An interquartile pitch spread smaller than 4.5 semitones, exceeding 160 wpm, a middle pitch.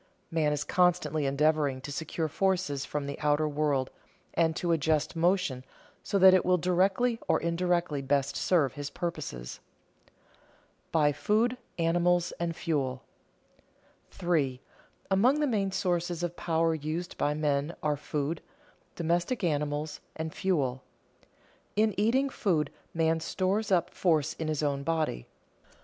No: average, 3.4 semitones; slow, 135 wpm; medium, 160 Hz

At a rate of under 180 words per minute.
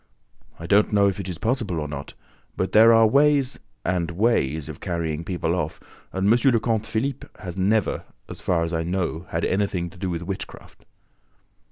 No: average, 190 wpm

